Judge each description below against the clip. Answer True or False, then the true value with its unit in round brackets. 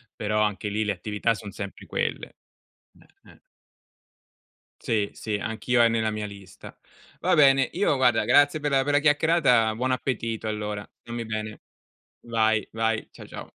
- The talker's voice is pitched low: True (110 Hz)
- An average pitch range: True (3.3 semitones)